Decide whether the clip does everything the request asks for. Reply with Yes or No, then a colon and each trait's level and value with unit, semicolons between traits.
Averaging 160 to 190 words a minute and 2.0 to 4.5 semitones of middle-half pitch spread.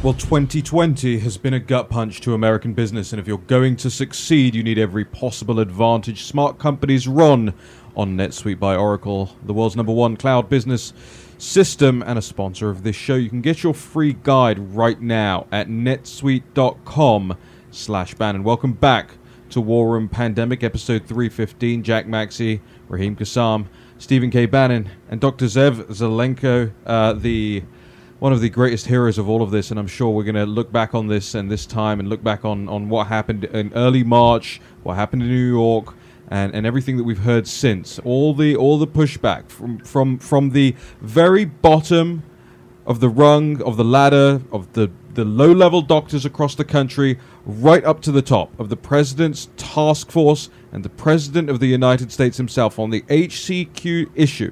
Yes: average, 185 wpm; average, 3.9 semitones